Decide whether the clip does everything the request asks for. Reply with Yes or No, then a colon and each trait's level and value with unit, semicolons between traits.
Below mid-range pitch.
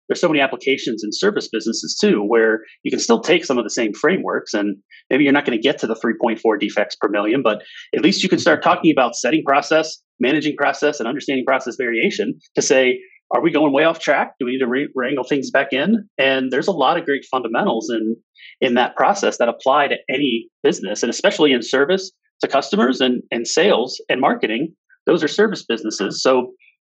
No: medium, 145 Hz